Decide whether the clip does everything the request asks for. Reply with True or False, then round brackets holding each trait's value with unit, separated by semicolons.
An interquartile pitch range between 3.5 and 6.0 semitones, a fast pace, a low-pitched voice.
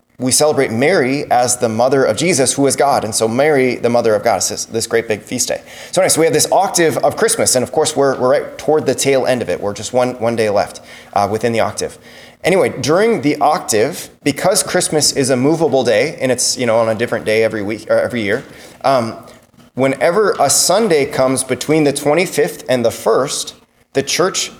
True (4.5 semitones; 225 wpm; 130 Hz)